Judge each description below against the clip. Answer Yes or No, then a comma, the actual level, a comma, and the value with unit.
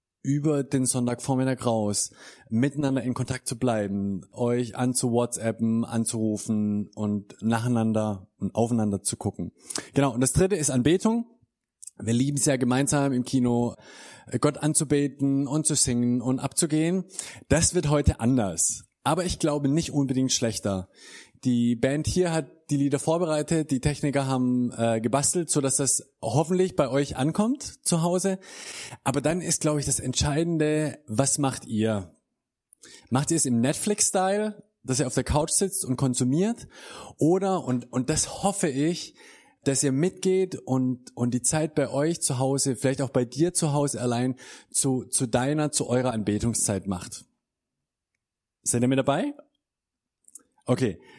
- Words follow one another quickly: No, average, 150 wpm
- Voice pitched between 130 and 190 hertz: Yes, low, 135 Hz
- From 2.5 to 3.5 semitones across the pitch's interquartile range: No, average, 4.2 semitones